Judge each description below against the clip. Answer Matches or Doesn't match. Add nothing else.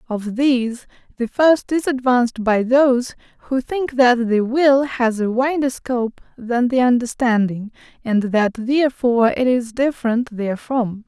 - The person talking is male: Doesn't match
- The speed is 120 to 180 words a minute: Matches